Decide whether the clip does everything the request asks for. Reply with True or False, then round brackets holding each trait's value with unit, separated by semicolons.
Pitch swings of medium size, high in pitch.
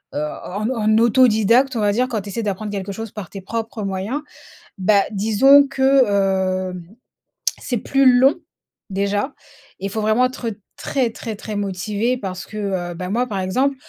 True (4.0 semitones; 215 Hz)